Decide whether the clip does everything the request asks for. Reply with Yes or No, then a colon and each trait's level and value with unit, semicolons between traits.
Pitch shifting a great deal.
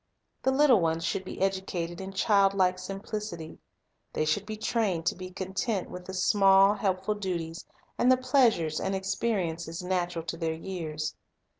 No: average, 3.2 semitones